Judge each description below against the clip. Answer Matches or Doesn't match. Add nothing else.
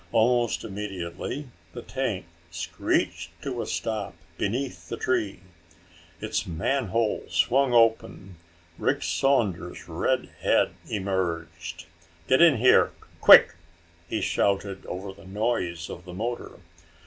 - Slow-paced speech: Matches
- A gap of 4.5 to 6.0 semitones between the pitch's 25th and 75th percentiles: Matches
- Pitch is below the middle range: Matches